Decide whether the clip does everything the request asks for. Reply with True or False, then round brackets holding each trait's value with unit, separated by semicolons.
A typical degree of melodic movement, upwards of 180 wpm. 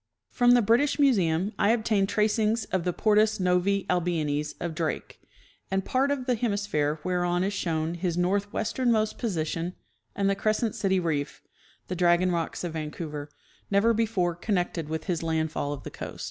False (4.5 semitones; 160 wpm)